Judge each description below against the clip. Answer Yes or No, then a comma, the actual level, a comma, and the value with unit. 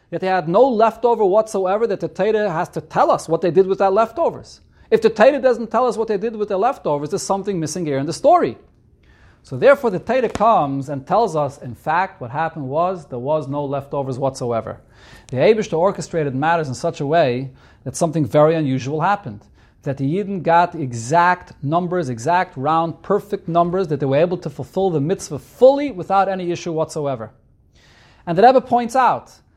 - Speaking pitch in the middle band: Yes, medium, 170 Hz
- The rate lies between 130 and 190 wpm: No, fast, 205 wpm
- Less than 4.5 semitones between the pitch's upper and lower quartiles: No, wide, 5.4 semitones